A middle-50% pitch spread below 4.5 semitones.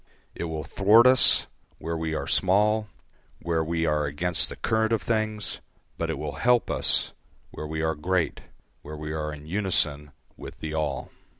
No: wide, 5.4 semitones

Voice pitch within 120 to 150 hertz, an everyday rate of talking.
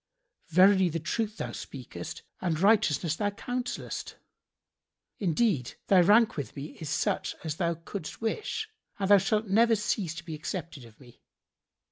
No: medium, 185 Hz; average, 150 wpm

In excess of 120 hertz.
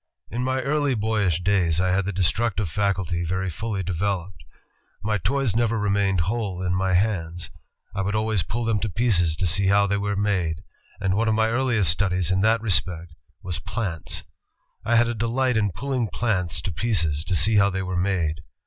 No: low, 100 Hz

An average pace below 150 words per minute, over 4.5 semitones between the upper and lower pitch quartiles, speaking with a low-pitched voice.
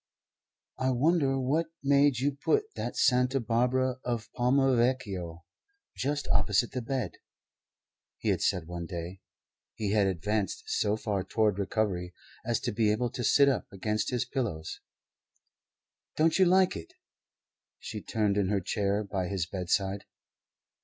Yes: average, 140 wpm; average, 4.9 semitones; low, 110 Hz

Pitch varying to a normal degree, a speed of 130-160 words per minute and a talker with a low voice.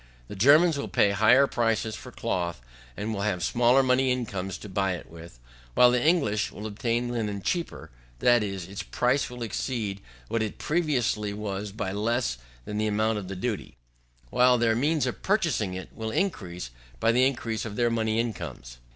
No: average, 3.7 semitones; average, 185 wpm; low, 110 Hz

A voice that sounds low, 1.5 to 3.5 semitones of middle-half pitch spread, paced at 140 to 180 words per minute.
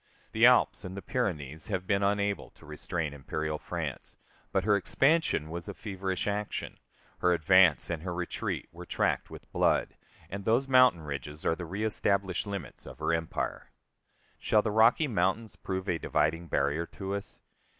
No: very low, 95 Hz; average, 3.9 semitones; average, 165 wpm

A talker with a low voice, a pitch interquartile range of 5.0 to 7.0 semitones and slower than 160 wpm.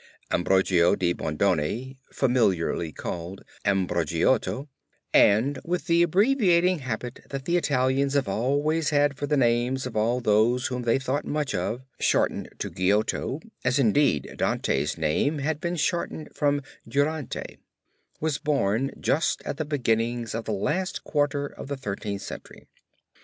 Yes: low, 130 Hz; wide, 5.6 semitones; average, 140 wpm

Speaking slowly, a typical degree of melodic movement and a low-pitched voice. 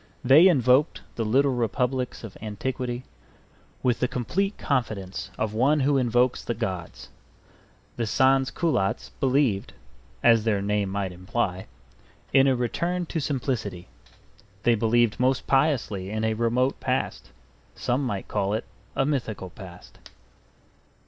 Yes: slow, 130 wpm; average, 4.2 semitones; low, 120 Hz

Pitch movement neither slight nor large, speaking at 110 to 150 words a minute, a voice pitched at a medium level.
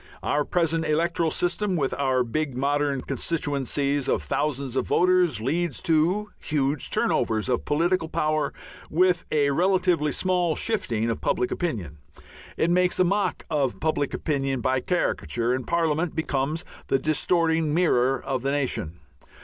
Yes: average, 4.2 semitones; average, 140 wpm; medium, 150 Hz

